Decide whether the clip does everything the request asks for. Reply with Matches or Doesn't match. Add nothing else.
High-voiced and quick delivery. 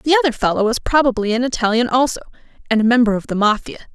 Matches